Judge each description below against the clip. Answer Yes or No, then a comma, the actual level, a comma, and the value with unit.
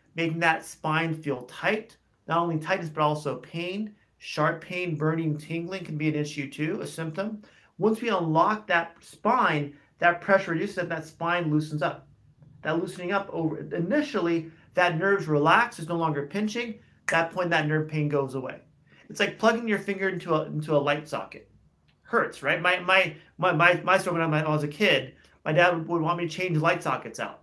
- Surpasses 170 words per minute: Yes, average, 195 wpm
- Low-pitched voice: No, medium, 165 Hz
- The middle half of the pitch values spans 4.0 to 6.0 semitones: No, average, 3.1 semitones